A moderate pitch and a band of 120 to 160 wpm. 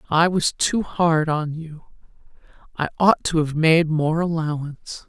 Yes: medium, 160 Hz; average, 140 wpm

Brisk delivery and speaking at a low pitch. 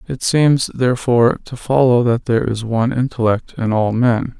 No: average, 180 wpm; low, 120 Hz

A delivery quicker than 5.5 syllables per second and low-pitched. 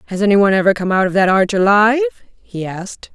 No: 6.3 syllables/s; high, 205 Hz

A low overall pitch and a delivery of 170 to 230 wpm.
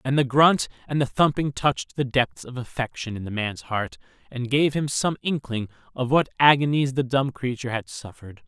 Yes: low, 125 Hz; average, 200 wpm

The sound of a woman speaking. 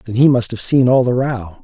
No: male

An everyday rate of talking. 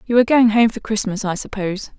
No: fast, 240 wpm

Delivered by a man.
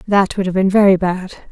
No: female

